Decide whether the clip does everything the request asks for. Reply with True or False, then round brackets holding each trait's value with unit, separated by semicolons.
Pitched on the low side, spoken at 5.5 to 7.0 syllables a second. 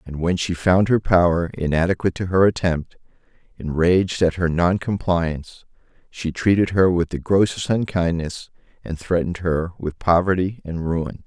False (90 Hz; 4.9 syllables/s)